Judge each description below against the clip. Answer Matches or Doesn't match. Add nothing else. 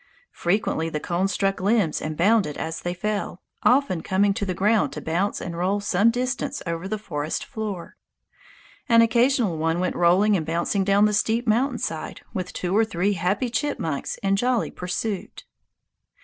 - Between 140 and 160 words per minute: Doesn't match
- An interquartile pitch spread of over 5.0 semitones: Doesn't match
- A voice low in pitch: Doesn't match